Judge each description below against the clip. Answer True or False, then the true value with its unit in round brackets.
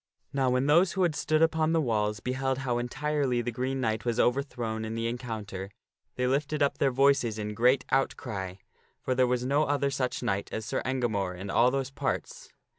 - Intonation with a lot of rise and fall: False (3.6 semitones)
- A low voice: True (125 Hz)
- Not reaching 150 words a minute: False (195 wpm)